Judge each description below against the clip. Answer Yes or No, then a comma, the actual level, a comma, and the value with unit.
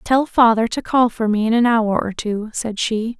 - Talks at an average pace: No, fast, 245 wpm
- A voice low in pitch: No, high, 230 Hz